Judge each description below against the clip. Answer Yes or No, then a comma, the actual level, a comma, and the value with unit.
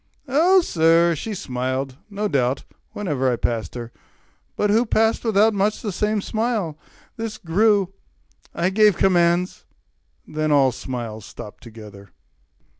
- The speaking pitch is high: No, medium, 175 Hz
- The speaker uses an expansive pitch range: Yes, wide, 8.5 semitones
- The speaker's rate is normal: No, slow, 130 wpm